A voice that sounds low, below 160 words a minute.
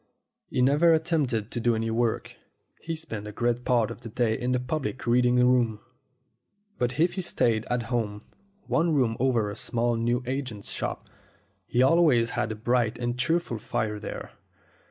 No: low, 120 Hz; average, 175 wpm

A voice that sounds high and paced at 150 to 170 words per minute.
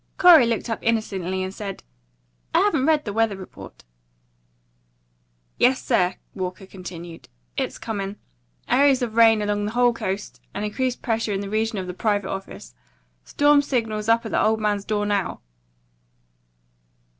Yes: high, 215 Hz; average, 155 wpm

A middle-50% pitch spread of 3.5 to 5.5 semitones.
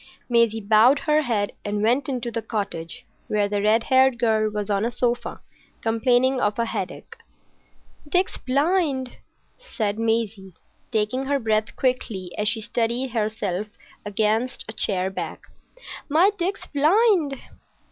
Yes: average, 3.8 semitones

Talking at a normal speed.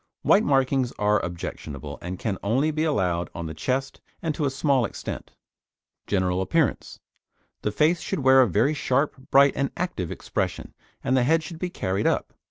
Yes: average, 180 wpm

